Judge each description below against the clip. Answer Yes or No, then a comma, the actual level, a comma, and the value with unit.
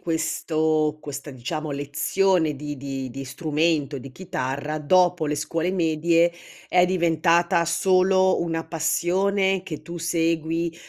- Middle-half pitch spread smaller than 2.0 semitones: No, average, 2.7 semitones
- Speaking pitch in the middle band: Yes, medium, 165 Hz